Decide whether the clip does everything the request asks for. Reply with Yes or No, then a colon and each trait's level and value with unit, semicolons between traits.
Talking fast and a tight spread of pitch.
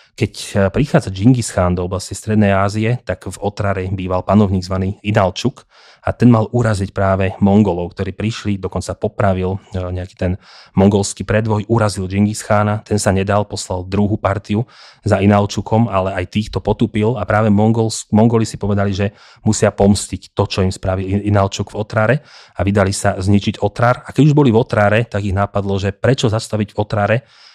Yes: fast, 170 wpm; narrow, 2.1 semitones